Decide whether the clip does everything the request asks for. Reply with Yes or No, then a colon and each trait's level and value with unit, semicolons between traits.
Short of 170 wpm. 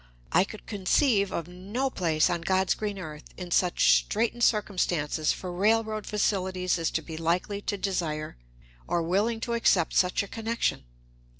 Yes: average, 160 wpm